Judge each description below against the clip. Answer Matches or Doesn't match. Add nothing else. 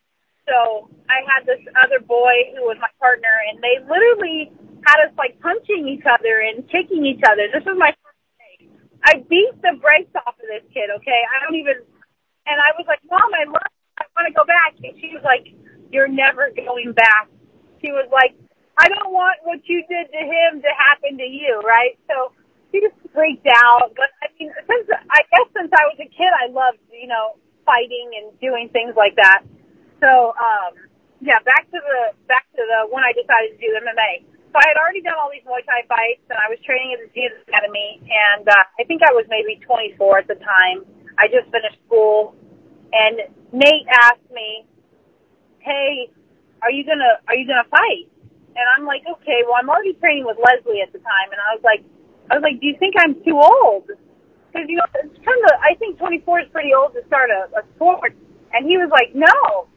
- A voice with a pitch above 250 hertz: Matches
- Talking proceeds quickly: Matches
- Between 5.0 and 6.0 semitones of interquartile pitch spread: Matches